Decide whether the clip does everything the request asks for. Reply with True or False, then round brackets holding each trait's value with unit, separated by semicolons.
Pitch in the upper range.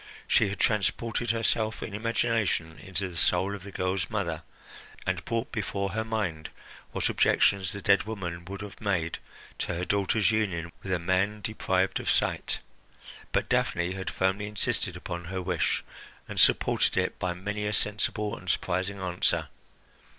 False (100 Hz)